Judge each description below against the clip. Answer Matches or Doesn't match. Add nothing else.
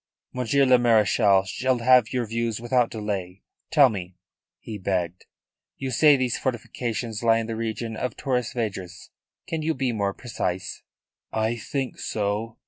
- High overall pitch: Doesn't match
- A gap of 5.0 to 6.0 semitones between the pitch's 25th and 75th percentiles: Doesn't match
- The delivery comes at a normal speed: Matches